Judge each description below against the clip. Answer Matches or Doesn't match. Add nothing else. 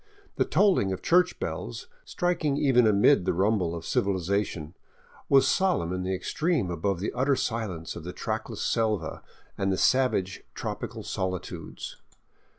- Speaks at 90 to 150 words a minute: Matches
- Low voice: Matches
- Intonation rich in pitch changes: Matches